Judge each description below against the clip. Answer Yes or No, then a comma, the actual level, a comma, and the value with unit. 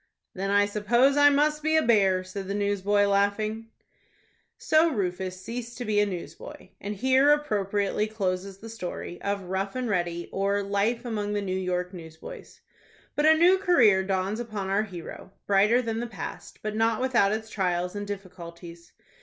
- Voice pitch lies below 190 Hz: No, high, 205 Hz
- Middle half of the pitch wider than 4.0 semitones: No, average, 3.4 semitones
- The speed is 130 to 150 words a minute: No, average, 170 wpm